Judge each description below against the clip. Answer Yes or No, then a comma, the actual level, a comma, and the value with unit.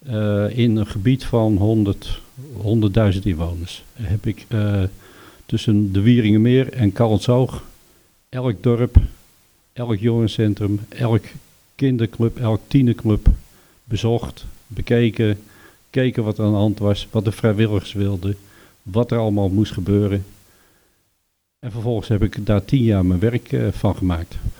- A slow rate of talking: Yes, slow, 130 wpm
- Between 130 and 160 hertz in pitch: No, low, 105 Hz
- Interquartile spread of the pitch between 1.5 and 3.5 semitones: Yes, narrow, 2.5 semitones